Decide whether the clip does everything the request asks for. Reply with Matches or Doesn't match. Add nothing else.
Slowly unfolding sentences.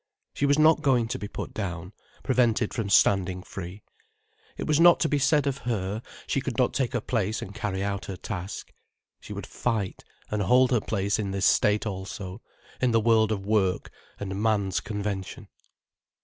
Doesn't match